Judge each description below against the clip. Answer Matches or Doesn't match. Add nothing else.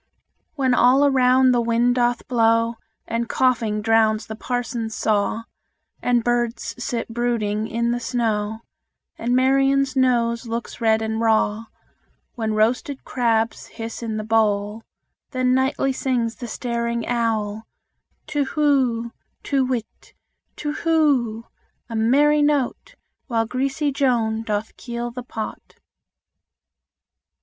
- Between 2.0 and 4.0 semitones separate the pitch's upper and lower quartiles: Matches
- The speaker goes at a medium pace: Doesn't match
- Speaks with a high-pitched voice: Matches